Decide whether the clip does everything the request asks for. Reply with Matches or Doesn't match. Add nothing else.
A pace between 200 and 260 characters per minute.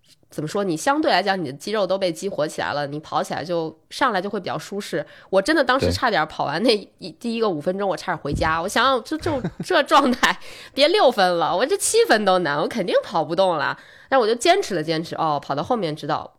Doesn't match